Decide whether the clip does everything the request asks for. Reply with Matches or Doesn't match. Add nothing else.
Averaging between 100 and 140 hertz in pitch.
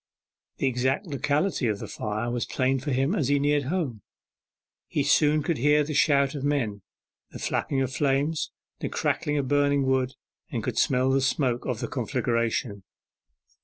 Matches